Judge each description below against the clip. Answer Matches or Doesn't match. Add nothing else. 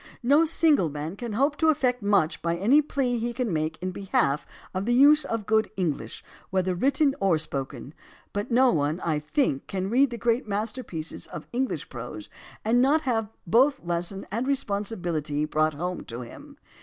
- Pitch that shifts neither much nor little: Doesn't match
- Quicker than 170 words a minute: Matches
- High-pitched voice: Matches